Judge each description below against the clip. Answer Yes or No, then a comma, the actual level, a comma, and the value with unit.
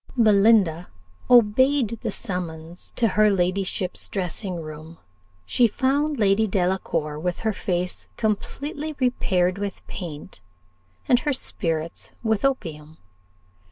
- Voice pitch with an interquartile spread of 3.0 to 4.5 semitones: No, average, 4.9 semitones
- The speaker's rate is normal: No, slow, 110 wpm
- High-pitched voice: Yes, high, 195 Hz